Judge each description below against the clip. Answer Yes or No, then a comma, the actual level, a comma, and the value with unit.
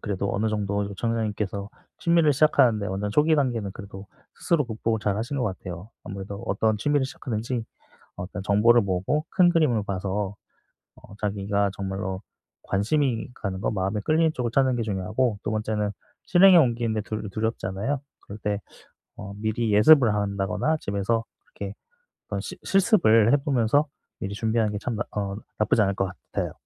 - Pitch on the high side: No, low, 110 Hz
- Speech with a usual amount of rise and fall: Yes, average, 3.8 semitones